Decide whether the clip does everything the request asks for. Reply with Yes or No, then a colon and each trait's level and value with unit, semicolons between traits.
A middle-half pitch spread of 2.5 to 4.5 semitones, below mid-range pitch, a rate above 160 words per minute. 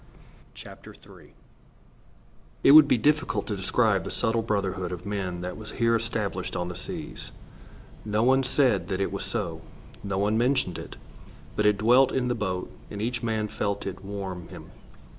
Yes: average, 3.5 semitones; low, 105 Hz; average, 170 wpm